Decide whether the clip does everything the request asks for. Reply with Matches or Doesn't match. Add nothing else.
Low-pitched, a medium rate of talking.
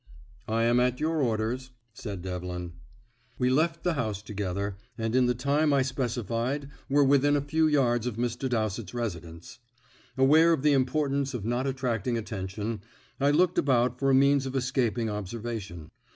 Matches